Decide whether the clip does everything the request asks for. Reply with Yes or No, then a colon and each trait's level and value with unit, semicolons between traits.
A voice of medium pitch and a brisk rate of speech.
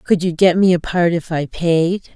Yes: medium, 175 Hz; fast, 250 wpm